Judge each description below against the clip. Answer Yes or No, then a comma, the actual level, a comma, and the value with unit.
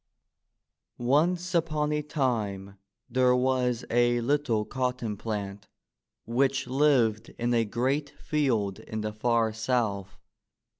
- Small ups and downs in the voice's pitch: No, average, 4.0 semitones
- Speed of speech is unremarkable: No, slow, 110 wpm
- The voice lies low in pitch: Yes, low, 120 Hz